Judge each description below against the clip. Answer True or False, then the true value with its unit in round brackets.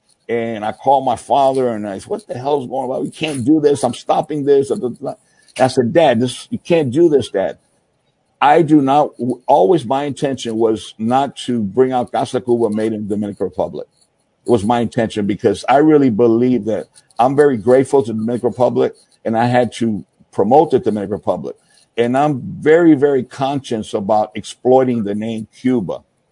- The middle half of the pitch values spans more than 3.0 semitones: True (3.7 semitones)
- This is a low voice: True (125 Hz)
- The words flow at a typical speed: True (190 wpm)